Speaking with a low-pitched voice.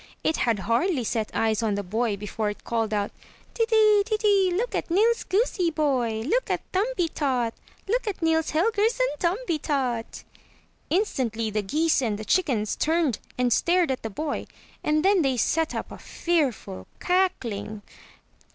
No: very high, 300 Hz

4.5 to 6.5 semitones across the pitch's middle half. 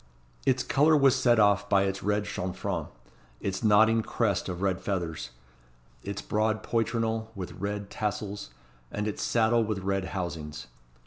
No: narrow, 2.5 semitones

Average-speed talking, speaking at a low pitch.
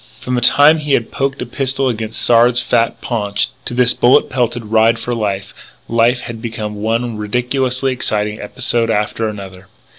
Yes: average, 170 wpm; low, 115 Hz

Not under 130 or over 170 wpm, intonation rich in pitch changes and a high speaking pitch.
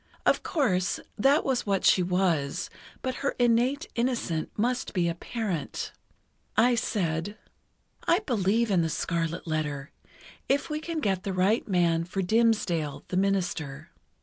Yes: average, 140 wpm; wide, 6.1 semitones; high, 195 Hz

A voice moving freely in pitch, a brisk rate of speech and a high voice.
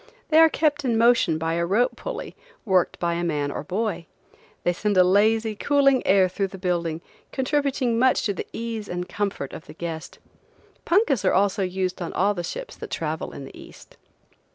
No: wide, 5.9 semitones; average, 195 wpm; high, 195 Hz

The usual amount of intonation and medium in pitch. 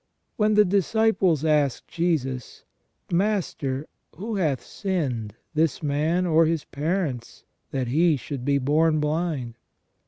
Yes: average, 4.4 semitones; medium, 155 Hz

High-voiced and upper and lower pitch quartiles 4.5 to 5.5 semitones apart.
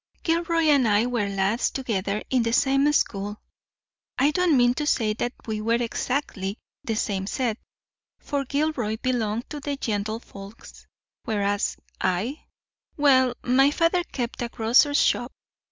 Yes: high, 245 Hz; average, 4.8 semitones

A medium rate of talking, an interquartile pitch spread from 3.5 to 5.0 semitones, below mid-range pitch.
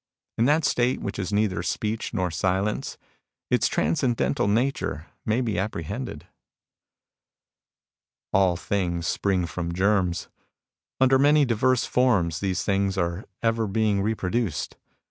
No: slow, 125 wpm; average, 4.1 semitones; low, 100 Hz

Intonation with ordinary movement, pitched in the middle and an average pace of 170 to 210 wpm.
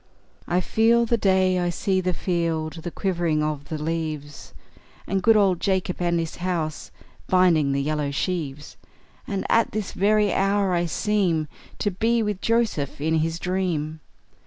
No: average, 3.8 semitones; medium, 175 Hz; average, 160 wpm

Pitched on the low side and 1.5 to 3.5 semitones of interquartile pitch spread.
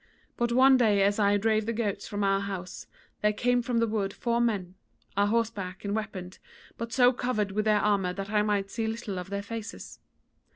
No: high, 210 Hz; narrow, 2.6 semitones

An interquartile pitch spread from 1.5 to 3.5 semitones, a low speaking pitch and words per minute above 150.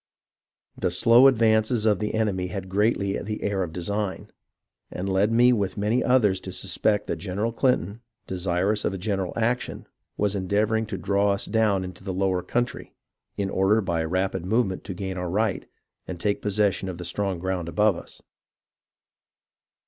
Yes: average, 2.7 semitones; low, 100 Hz; average, 170 wpm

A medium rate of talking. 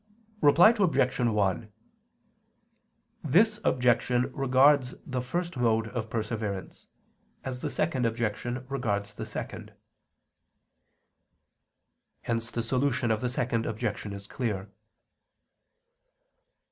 No: slow, 95 wpm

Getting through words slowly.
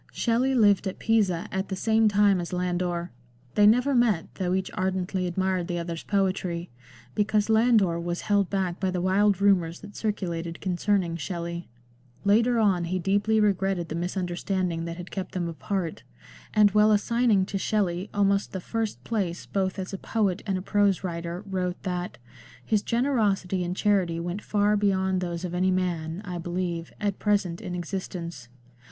No: average, 170 wpm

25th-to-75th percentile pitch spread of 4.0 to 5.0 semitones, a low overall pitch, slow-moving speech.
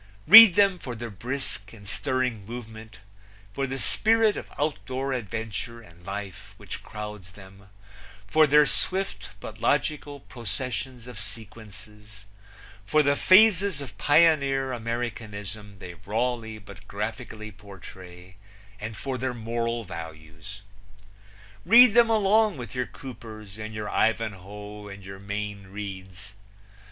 Yes: average, 4.6 semitones; low, 110 Hz; slow, 125 wpm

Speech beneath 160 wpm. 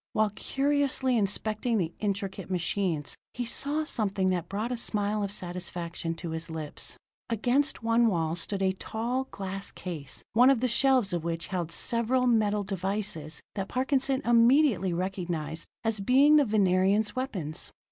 Yes: average, 150 wpm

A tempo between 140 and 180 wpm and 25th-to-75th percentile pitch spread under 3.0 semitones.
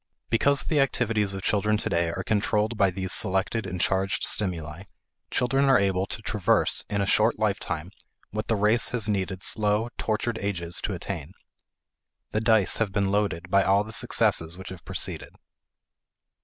Yes: average, 165 wpm; narrow, 2.6 semitones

